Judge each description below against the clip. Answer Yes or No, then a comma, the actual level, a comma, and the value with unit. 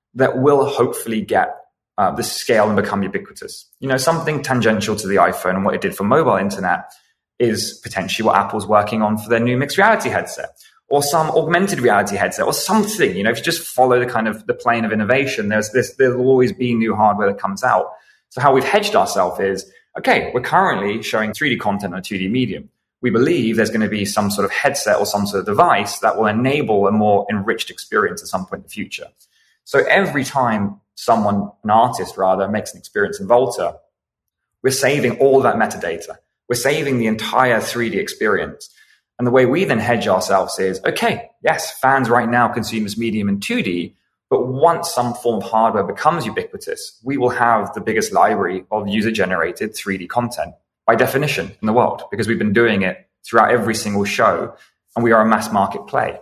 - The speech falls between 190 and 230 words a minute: Yes, fast, 205 wpm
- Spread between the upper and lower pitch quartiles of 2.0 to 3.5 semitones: No, average, 4.2 semitones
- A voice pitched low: Yes, low, 115 Hz